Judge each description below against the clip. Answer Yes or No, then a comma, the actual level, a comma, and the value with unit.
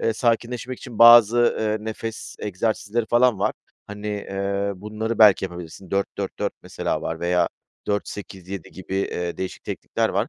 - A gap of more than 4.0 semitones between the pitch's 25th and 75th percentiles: No, average, 2.9 semitones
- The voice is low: Yes, low, 105 Hz